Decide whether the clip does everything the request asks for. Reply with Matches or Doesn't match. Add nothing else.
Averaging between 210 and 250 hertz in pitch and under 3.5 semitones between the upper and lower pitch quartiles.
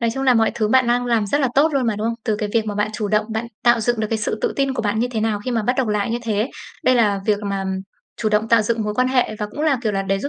Matches